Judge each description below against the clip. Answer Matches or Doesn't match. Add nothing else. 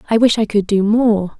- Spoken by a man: Doesn't match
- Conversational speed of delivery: Doesn't match